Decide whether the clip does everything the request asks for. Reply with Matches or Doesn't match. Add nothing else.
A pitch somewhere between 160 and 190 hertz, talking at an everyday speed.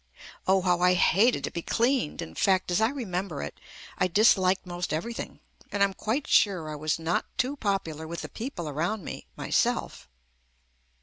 Matches